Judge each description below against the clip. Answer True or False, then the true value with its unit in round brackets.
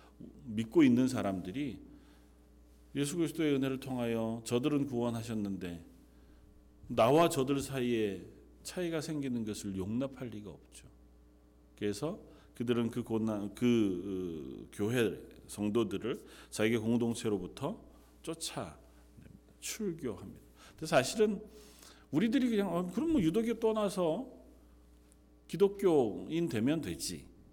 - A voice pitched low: True (115 Hz)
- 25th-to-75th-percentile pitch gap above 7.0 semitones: True (8.6 semitones)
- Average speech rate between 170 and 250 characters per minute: True (245 characters per minute)